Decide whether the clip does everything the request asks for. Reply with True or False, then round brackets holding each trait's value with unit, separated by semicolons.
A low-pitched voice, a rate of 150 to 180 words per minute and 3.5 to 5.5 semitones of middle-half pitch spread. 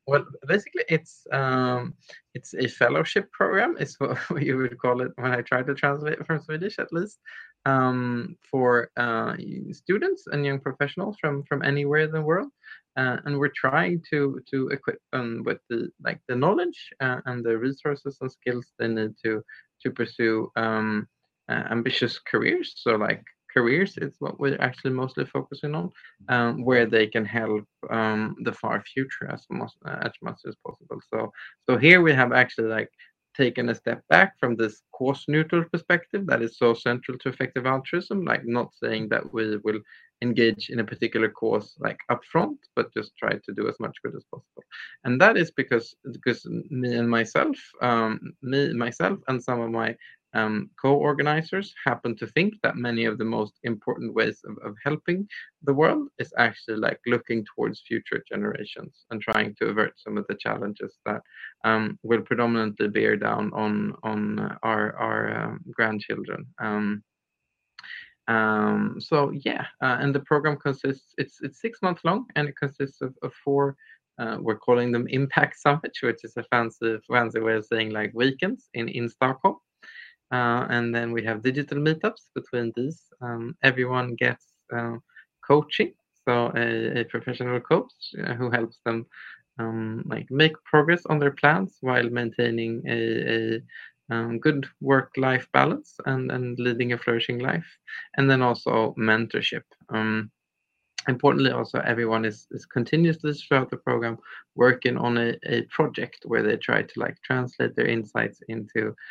True (125 Hz; 170 wpm; 4.0 semitones)